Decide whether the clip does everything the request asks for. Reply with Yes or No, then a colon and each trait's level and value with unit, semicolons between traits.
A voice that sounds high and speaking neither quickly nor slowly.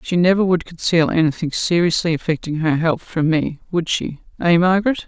No: medium, 165 Hz; average, 175 wpm